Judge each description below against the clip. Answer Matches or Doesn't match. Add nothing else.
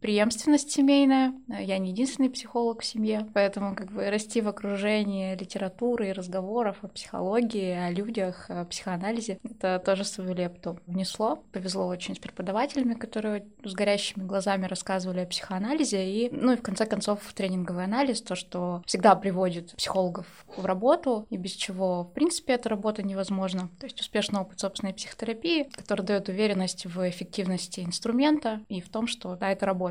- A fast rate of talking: Matches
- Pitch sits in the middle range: Doesn't match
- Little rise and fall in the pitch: Doesn't match